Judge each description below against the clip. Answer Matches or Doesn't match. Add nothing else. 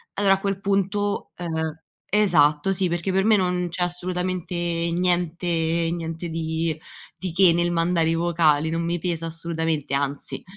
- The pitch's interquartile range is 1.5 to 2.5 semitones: Matches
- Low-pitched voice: Doesn't match